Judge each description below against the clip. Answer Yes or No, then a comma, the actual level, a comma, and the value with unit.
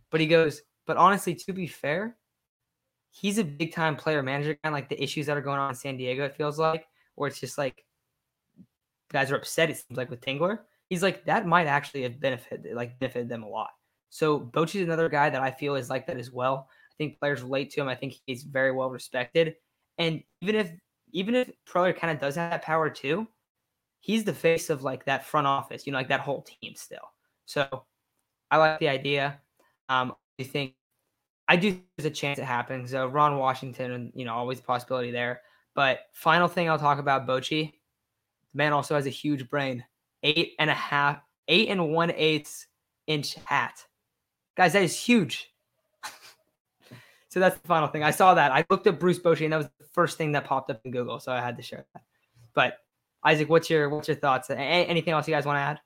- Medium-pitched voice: Yes, medium, 145 Hz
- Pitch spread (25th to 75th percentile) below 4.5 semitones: Yes, average, 3.9 semitones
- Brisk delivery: Yes, fast, 220 wpm